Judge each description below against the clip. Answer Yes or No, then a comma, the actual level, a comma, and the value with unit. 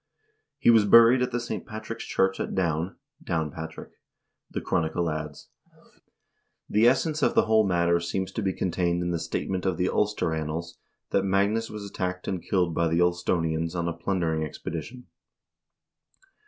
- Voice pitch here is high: No, very low, 90 Hz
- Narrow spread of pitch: No, average, 3.6 semitones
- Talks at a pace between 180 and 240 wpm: No, average, 165 wpm